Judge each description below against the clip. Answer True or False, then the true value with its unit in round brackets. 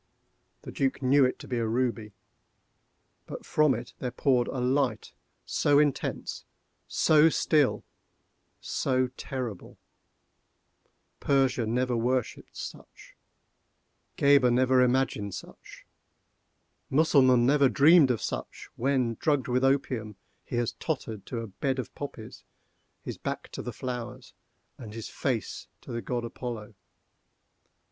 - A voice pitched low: True (125 Hz)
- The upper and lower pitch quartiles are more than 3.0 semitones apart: False (2.5 semitones)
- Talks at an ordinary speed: False (120 wpm)